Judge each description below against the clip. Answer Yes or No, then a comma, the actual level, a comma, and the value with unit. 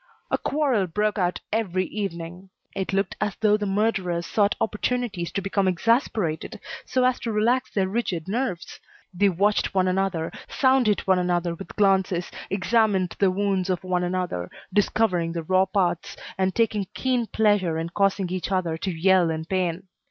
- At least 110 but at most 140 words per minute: No, average, 165 wpm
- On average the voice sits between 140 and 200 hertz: Yes, high, 190 Hz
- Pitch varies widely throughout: No, average, 3.0 semitones